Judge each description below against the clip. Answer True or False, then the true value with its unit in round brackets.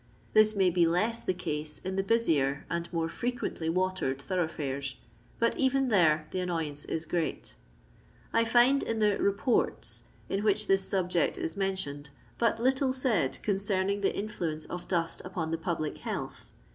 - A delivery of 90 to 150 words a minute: False (165 wpm)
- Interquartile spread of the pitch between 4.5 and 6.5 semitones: True (4.8 semitones)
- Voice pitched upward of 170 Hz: True (185 Hz)